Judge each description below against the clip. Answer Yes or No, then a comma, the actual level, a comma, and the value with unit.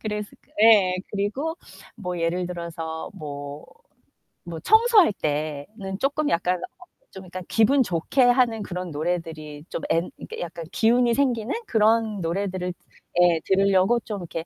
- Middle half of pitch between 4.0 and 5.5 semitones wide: Yes, average, 5.2 semitones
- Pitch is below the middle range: No, medium, 185 Hz